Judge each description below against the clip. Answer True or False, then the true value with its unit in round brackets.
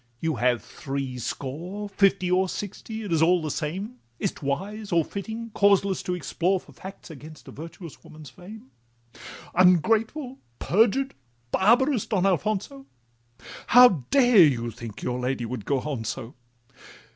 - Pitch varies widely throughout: True (6.7 semitones)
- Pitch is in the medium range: True (180 Hz)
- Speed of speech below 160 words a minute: True (145 wpm)